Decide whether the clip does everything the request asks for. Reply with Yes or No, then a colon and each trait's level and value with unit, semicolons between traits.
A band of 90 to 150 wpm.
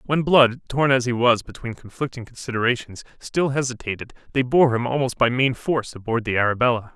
No: average, 180 wpm